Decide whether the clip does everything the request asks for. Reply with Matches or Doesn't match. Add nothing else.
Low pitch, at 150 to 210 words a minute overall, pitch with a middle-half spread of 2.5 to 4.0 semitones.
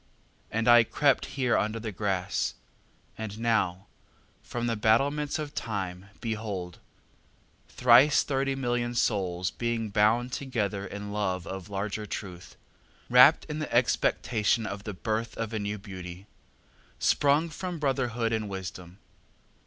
Doesn't match